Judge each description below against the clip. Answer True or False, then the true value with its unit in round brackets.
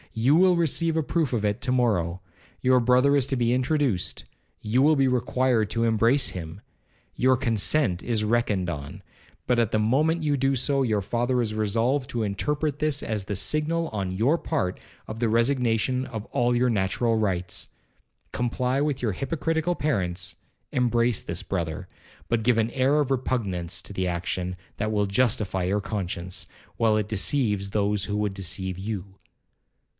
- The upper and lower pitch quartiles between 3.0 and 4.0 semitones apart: False (4.8 semitones)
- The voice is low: True (115 Hz)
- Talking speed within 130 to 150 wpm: False (165 wpm)